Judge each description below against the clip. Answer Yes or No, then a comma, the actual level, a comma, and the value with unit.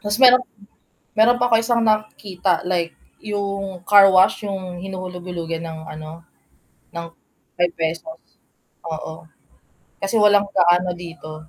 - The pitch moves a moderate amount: Yes, average, 3.5 semitones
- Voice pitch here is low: No, medium, 185 Hz